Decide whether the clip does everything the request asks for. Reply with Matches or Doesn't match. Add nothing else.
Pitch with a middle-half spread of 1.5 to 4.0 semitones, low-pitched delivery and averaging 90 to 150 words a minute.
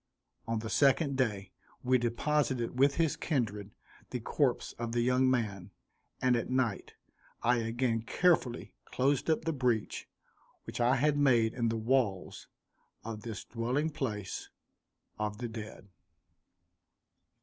Matches